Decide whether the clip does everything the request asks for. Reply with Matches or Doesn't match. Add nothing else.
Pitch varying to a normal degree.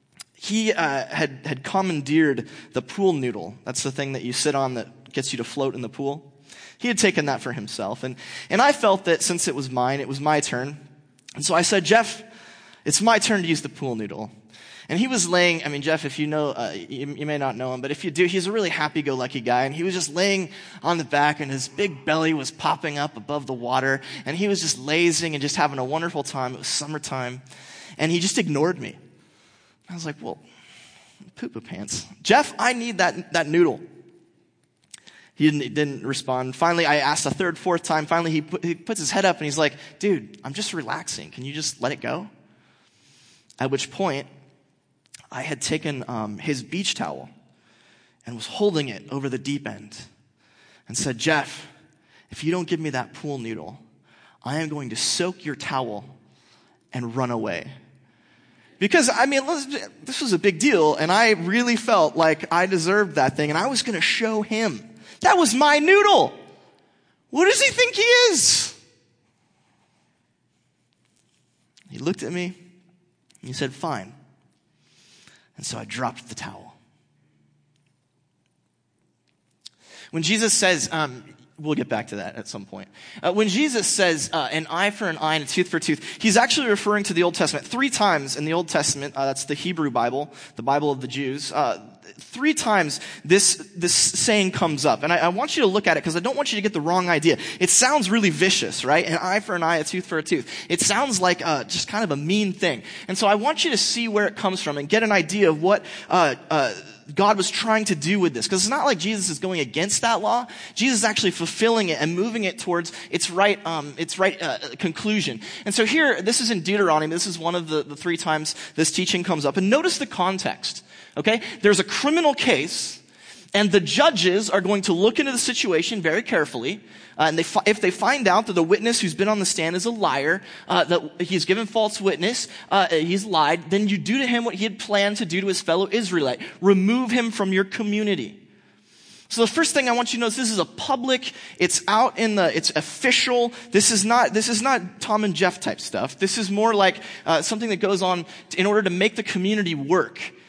Doesn't match